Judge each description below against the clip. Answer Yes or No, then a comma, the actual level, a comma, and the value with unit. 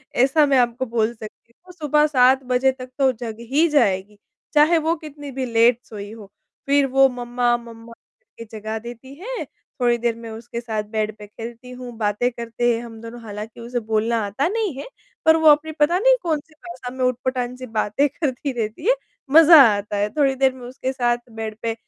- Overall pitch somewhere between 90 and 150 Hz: No, high, 245 Hz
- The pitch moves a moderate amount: Yes, average, 3.8 semitones